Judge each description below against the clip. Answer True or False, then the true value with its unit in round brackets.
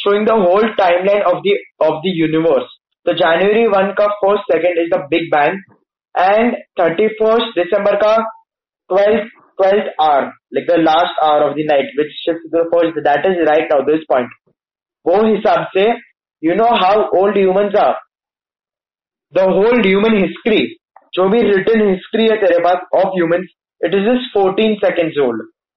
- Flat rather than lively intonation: False (3.9 semitones)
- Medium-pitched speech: False (195 Hz)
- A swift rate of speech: False (155 wpm)